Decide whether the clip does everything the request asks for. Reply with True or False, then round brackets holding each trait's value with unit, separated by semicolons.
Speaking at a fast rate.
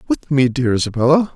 False (175 wpm)